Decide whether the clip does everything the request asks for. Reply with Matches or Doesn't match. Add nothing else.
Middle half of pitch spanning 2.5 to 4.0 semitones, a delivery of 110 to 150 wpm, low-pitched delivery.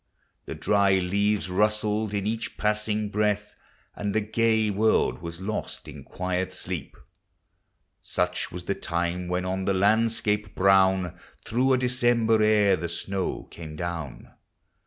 Matches